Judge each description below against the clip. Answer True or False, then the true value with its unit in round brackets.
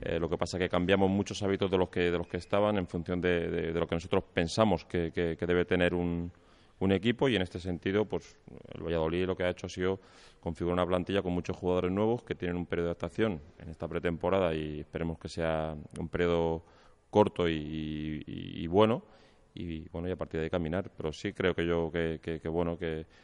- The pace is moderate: False (235 wpm)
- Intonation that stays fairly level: True (2.2 semitones)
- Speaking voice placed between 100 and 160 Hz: False (90 Hz)